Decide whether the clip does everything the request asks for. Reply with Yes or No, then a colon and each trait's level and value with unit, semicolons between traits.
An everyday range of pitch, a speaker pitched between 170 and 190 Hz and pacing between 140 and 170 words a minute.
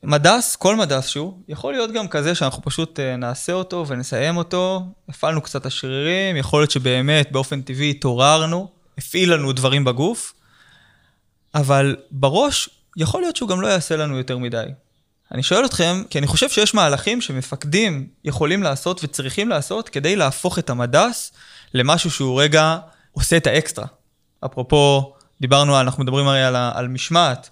No: average, 4.7 semitones; medium, 150 Hz; fast, 150 wpm